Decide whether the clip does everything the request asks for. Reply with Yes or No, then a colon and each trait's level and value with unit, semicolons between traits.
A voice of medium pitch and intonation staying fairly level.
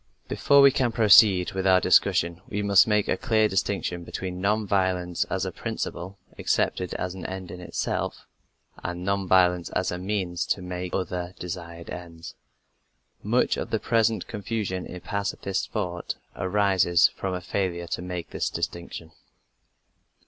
No: very low, 95 Hz; narrow, 2.2 semitones